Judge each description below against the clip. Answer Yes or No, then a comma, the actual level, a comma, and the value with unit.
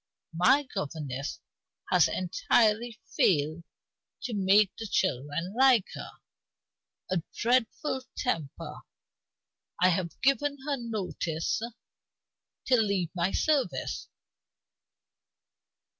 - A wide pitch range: Yes, wide, 6.4 semitones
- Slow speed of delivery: Yes, slow, 85 wpm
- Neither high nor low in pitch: No, high, 195 Hz